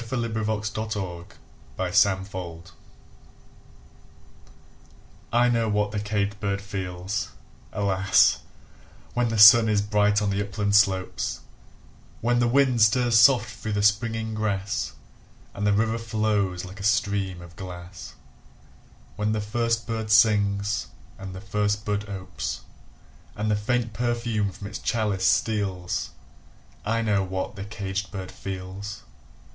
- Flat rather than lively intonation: Yes, narrow, 2.1 semitones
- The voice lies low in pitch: Yes, low, 105 Hz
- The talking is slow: Yes, slow, 130 wpm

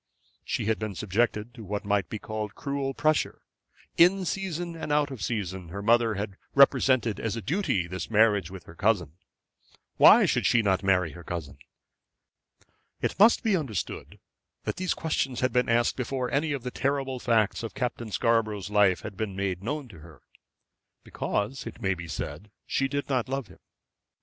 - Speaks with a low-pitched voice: Yes, low, 115 Hz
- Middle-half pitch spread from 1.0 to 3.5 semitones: No, wide, 5.4 semitones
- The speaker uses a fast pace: No, average, 180 wpm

